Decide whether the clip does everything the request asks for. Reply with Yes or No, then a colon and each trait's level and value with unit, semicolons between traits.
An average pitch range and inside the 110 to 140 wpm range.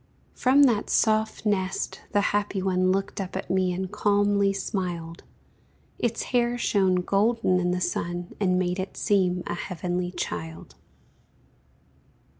No: narrow, 2.3 semitones; slow, 135 wpm